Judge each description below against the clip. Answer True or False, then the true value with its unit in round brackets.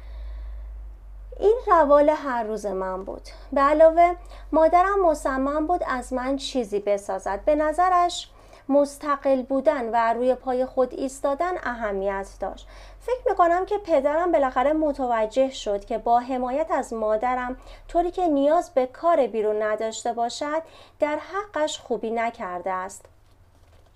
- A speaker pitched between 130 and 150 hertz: False (265 Hz)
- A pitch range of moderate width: False (6.5 semitones)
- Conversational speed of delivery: True (130 wpm)